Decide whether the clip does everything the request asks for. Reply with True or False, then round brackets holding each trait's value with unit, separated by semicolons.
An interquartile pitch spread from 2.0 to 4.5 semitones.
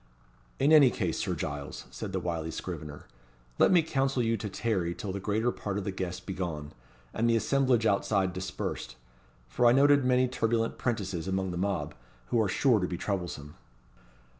False (5.0 semitones)